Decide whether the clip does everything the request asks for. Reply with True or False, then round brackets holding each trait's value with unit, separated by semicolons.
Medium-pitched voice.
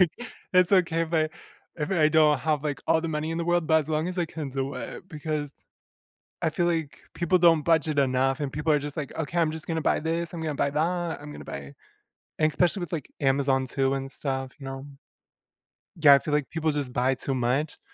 True (155 Hz)